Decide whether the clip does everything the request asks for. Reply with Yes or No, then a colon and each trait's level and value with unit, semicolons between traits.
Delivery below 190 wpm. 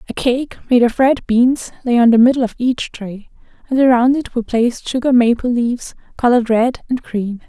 No: average, 200 wpm